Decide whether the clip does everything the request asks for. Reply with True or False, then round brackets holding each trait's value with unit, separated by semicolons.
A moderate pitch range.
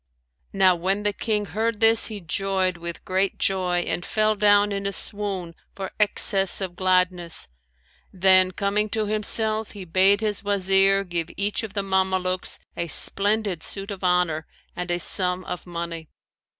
False (2.3 semitones)